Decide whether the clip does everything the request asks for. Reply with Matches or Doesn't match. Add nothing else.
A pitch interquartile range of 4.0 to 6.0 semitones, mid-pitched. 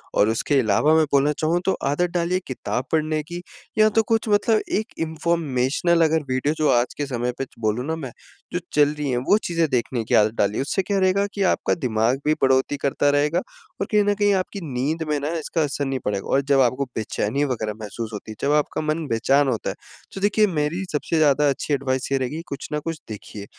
Matches